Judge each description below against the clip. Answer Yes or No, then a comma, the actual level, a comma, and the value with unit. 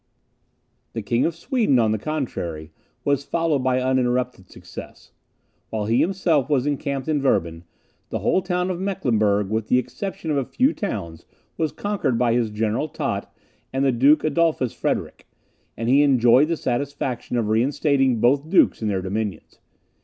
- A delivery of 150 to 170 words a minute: Yes, average, 160 wpm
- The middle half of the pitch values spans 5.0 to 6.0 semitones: Yes, average, 5.3 semitones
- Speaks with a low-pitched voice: Yes, low, 130 Hz